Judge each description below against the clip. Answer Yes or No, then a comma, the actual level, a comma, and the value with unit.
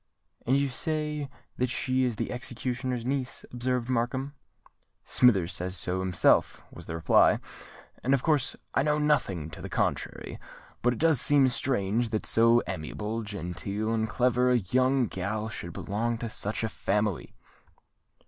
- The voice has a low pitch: Yes, low, 120 Hz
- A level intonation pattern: No, average, 4.0 semitones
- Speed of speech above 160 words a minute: No, average, 155 wpm